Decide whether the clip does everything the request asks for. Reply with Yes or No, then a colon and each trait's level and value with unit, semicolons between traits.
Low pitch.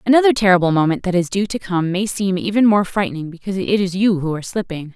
No: high, 190 Hz